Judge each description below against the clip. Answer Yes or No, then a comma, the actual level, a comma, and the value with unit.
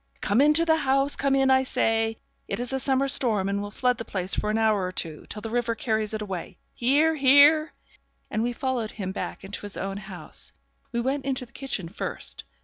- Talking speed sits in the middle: No, fast, 220 wpm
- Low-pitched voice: No, high, 235 Hz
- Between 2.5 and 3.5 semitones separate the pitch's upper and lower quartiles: No, average, 4.7 semitones